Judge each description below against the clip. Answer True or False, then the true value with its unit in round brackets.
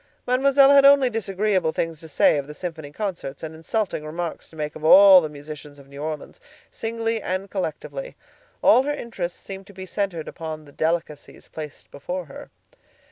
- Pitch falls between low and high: True (175 Hz)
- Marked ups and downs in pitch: True (5.7 semitones)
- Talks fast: False (180 wpm)